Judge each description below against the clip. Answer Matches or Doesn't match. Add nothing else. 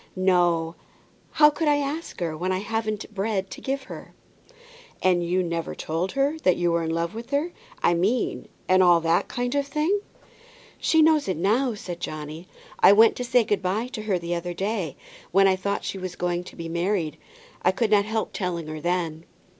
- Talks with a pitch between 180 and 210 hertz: Matches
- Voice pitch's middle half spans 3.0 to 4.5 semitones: Doesn't match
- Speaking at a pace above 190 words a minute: Matches